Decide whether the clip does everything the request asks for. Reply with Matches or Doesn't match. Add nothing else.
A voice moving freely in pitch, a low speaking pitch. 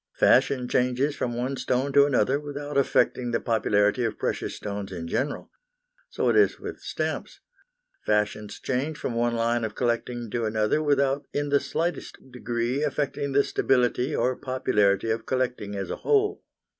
Doesn't match